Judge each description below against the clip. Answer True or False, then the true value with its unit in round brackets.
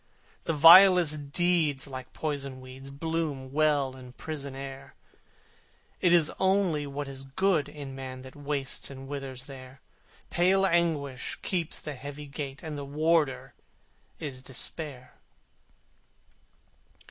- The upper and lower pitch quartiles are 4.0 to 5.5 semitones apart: False (3.2 semitones)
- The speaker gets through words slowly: True (125 wpm)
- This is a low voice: False (145 Hz)